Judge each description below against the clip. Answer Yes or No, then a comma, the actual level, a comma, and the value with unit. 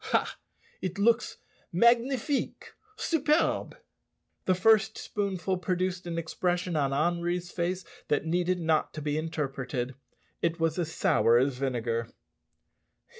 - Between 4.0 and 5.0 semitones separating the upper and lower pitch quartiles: No, average, 3.5 semitones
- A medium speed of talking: No, slow, 120 wpm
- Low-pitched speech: No, medium, 175 Hz